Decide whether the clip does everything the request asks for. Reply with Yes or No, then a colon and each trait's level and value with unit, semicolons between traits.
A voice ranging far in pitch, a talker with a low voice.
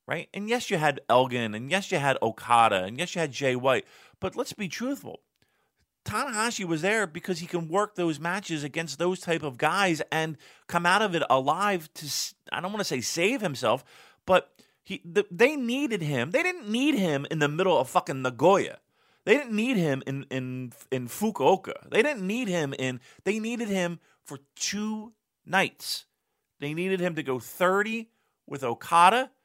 No: wide, 6.4 semitones; medium, 175 Hz